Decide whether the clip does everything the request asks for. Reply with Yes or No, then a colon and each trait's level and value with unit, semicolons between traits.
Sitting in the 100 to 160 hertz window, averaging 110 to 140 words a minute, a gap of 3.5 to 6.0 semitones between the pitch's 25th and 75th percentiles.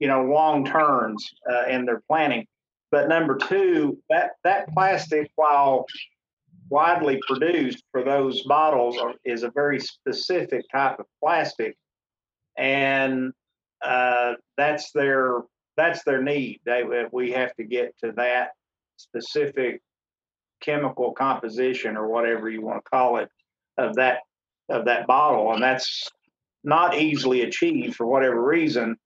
Yes: low, 135 Hz; slow, 135 wpm; average, 3.9 semitones